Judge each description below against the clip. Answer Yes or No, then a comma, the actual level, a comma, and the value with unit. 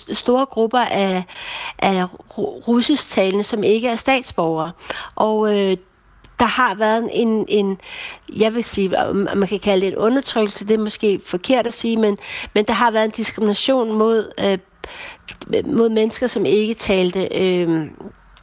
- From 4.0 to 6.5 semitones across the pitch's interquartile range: No, average, 3.2 semitones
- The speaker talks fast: No, average, 155 wpm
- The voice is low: No, high, 220 Hz